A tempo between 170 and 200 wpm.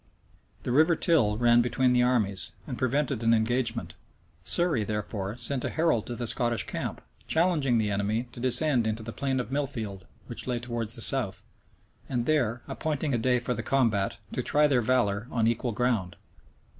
Yes: average, 180 wpm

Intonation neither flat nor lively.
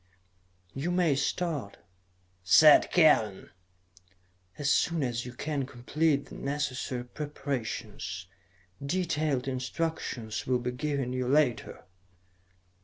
Yes: average, 3.6 semitones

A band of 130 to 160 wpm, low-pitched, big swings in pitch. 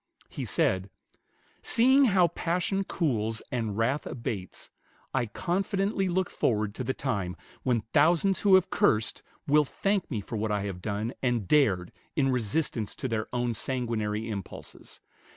Yes: average, 150 wpm; low, 125 Hz; wide, 8.1 semitones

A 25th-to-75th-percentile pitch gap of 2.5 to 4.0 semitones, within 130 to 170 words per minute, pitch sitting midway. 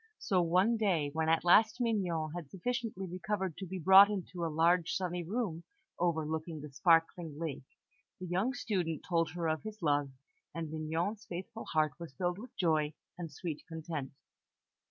Yes: average, 3.2 semitones; average, 165 wpm; medium, 170 Hz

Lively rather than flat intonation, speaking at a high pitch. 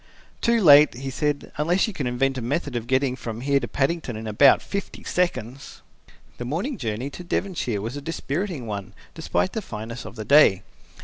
No: wide, 5.8 semitones; low, 135 Hz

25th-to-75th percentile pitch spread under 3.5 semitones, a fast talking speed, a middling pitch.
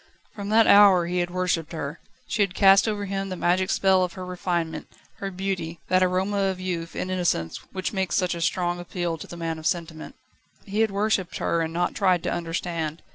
Yes: narrow, 2.4 semitones; fast, 210 wpm; medium, 180 Hz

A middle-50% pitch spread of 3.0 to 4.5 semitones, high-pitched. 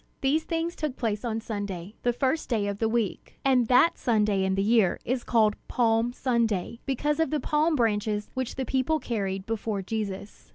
Yes: average, 4.0 semitones; high, 230 Hz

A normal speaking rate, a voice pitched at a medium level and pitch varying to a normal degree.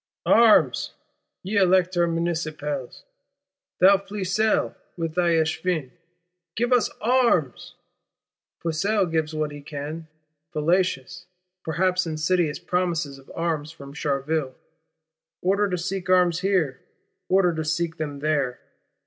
No: slow, 110 wpm; medium, 170 Hz; average, 3.3 semitones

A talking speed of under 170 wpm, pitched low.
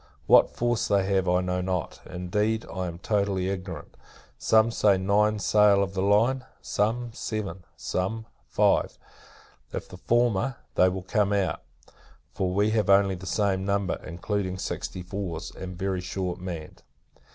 Yes: average, 150 wpm; very low, 95 Hz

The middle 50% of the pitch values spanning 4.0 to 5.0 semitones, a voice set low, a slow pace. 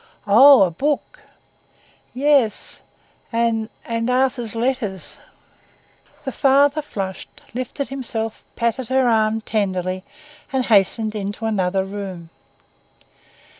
No: average, 4.6 semitones; high, 225 Hz; slow, 95 wpm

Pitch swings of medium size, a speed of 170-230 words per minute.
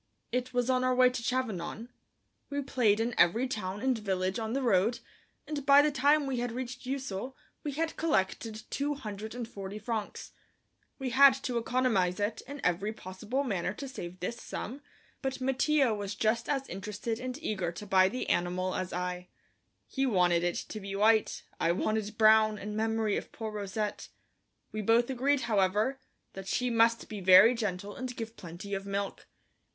Yes: average, 4.5 semitones; average, 175 wpm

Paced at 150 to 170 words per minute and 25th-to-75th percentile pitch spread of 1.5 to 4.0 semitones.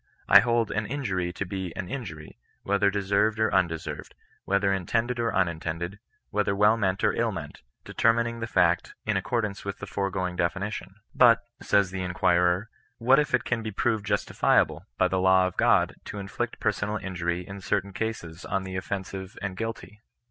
No: average, 185 wpm; average, 2.9 semitones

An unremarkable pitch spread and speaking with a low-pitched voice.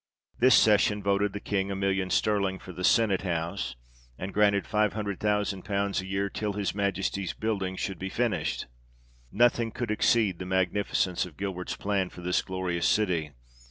No: narrow, 1.8 semitones; low, 100 Hz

